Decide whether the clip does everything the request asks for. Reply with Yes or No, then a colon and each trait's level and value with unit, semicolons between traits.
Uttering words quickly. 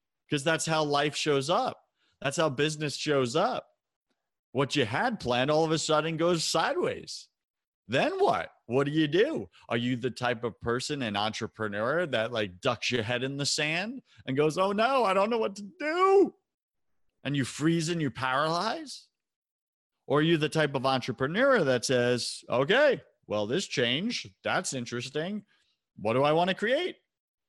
No: average, 175 wpm